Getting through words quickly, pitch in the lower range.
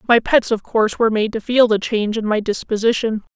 No: fast, 230 wpm; high, 220 Hz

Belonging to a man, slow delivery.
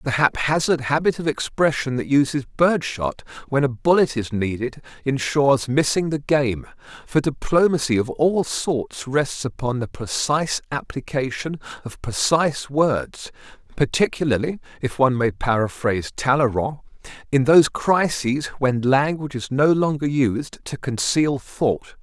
Yes: male; slow, 130 wpm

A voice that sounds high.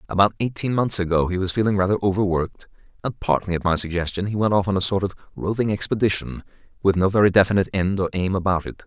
No: very low, 95 Hz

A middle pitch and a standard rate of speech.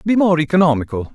Yes: medium, 165 Hz; average, 155 wpm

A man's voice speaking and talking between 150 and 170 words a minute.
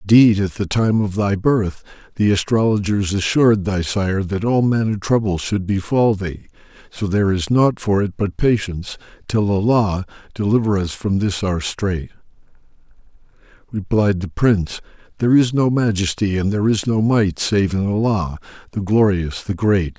Yes: male; average, 165 wpm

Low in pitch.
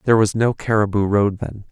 Yes: low, 105 Hz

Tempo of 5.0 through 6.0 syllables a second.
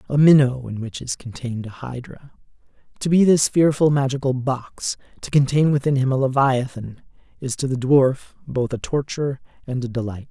Yes: 5.3 syllables/s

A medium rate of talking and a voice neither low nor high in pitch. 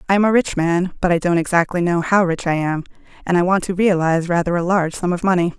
No: fast, 270 wpm; medium, 175 Hz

